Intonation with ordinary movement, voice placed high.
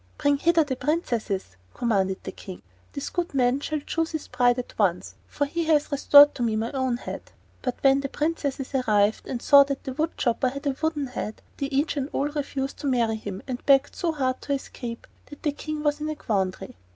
Yes: average, 3.5 semitones; very high, 275 Hz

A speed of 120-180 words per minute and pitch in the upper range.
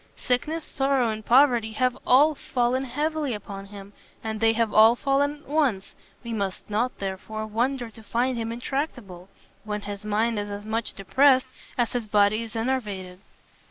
Yes: average, 165 wpm; high, 230 Hz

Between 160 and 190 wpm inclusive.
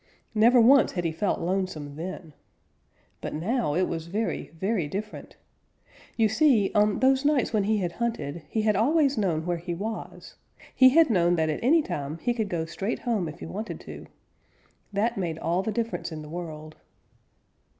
Yes: average, 180 wpm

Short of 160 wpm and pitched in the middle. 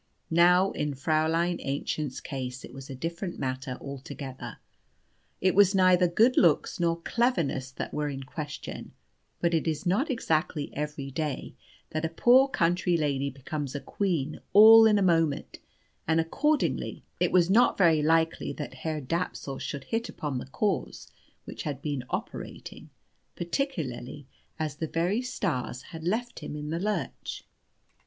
Yes: average, 150 wpm; medium, 160 Hz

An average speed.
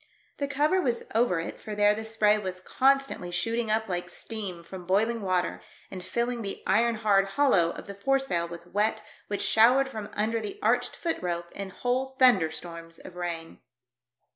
Yes: average, 175 wpm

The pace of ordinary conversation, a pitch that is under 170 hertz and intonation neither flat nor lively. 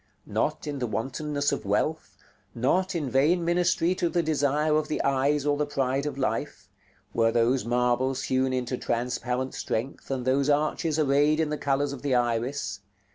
Yes: average, 175 wpm; medium, 140 Hz; average, 3.0 semitones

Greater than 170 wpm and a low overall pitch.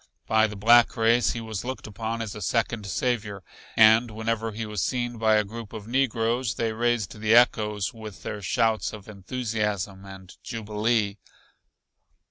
No: average, 160 wpm; low, 110 Hz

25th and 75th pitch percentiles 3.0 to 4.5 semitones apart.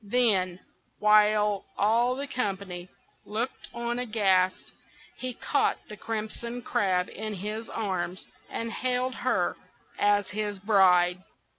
Yes: average, 3.6 semitones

